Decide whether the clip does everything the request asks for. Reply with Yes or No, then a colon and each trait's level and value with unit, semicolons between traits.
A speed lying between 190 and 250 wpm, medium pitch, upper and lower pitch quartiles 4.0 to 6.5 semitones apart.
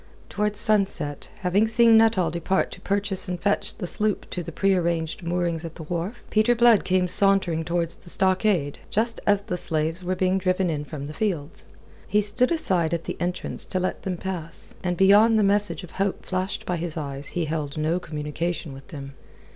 No: average, 195 wpm; medium, 180 Hz; average, 3.5 semitones